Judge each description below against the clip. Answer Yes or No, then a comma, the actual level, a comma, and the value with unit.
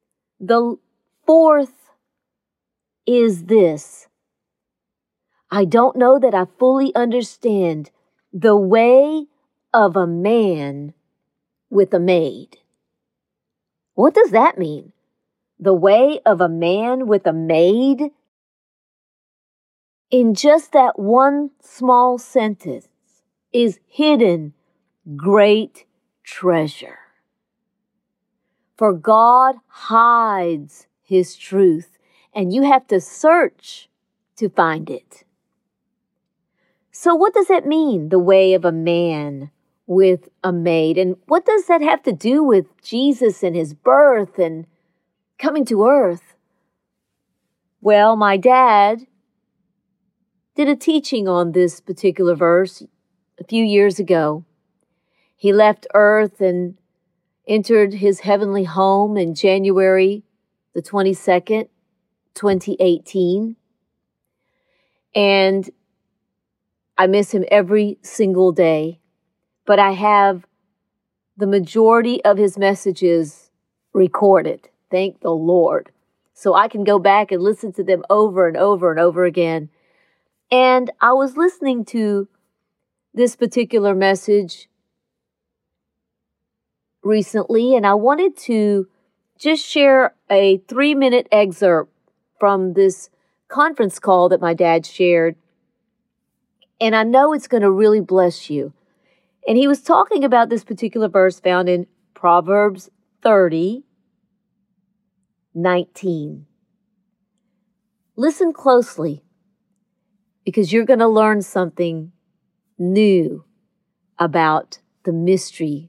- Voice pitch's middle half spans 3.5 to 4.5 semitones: Yes, average, 4.1 semitones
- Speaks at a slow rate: Yes, slow, 105 wpm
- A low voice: No, high, 200 Hz